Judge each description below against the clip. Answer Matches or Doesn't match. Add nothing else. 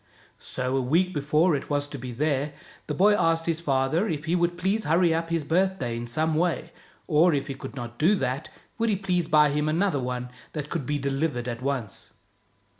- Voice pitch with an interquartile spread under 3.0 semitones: Doesn't match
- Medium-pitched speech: Matches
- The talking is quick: Matches